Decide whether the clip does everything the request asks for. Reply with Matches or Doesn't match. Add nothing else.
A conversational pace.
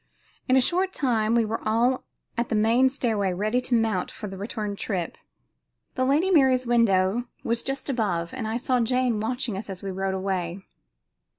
Matches